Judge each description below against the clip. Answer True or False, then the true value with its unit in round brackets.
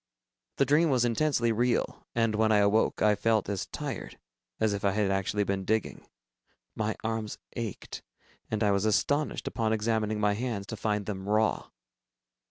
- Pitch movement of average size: False (1.9 semitones)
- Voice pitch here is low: True (110 Hz)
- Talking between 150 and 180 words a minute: True (170 wpm)